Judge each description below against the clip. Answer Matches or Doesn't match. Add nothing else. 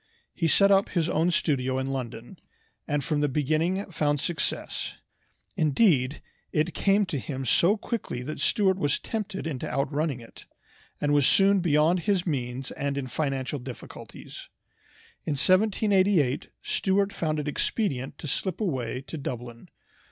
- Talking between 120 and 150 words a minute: Matches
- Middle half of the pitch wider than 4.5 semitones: Matches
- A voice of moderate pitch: Matches